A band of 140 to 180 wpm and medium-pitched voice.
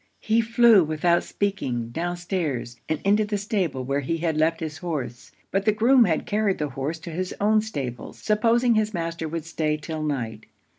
No: average, 190 wpm; medium, 170 Hz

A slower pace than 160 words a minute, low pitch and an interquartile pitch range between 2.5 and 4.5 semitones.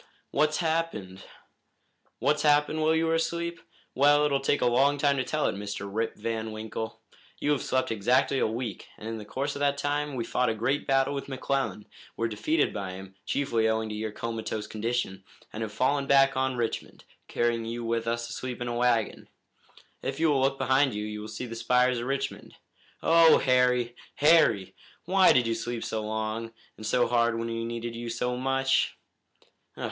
No: average, 195 wpm; low, 120 Hz; average, 3.7 semitones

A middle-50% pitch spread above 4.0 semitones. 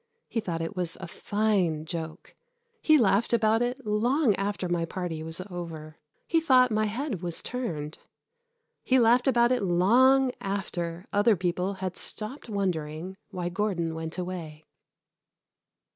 Yes: wide, 5.4 semitones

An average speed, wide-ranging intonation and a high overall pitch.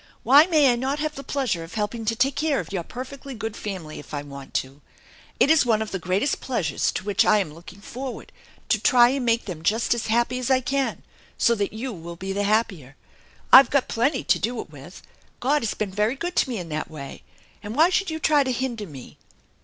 No: fast, 235 wpm; wide, 6.0 semitones; high, 225 Hz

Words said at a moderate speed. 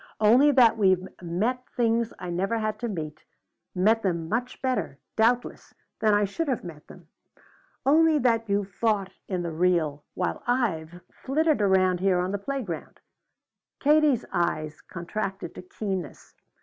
Yes: average, 150 wpm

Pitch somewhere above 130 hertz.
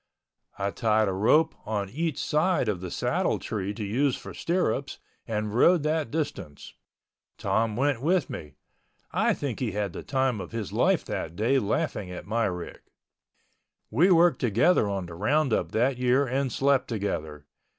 No: low, 115 Hz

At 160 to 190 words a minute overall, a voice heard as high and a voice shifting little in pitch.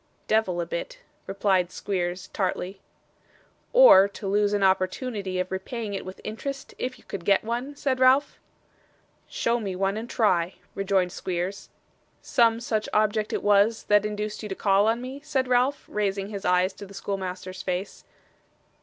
No: average, 165 wpm; high, 200 Hz; average, 3.3 semitones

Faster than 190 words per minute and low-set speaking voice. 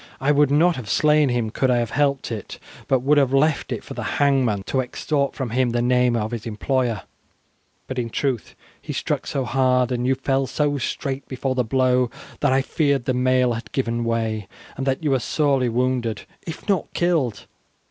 Yes: average, 200 wpm; low, 130 Hz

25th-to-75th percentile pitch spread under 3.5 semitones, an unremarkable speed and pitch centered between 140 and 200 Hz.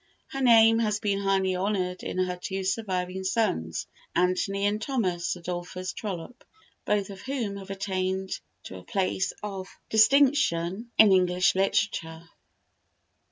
No: narrow, 2.5 semitones; slow, 130 wpm; high, 190 Hz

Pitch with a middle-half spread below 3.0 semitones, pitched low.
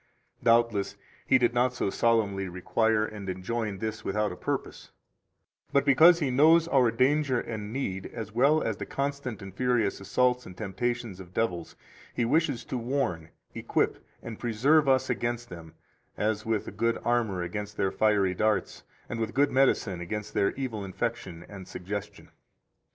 No: average, 4.2 semitones; low, 110 Hz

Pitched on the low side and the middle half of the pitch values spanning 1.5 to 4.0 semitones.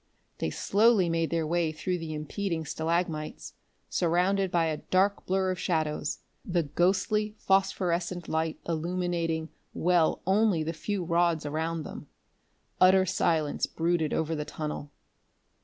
No: medium, 170 Hz; narrow, 2.6 semitones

